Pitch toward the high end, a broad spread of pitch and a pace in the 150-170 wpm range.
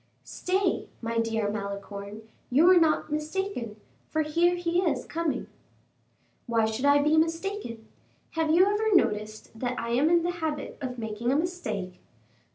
Yes: very high, 295 Hz; wide, 7.2 semitones; average, 155 wpm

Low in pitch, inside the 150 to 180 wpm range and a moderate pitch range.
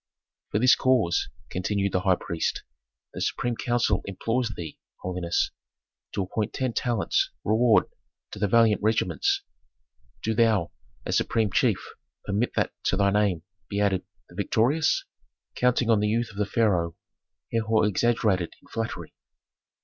No: low, 105 Hz; average, 140 wpm; average, 3.0 semitones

